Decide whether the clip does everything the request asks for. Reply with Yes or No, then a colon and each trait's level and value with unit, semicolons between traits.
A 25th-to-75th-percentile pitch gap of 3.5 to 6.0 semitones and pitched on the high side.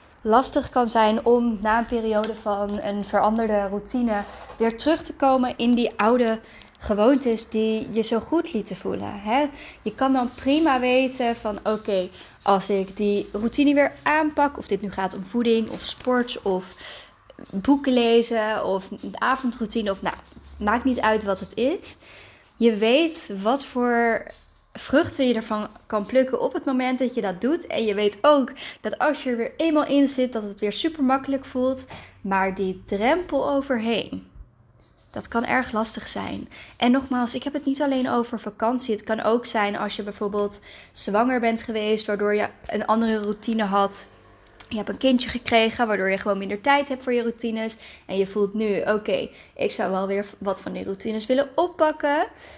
Yes: average, 3.8 semitones; high, 230 Hz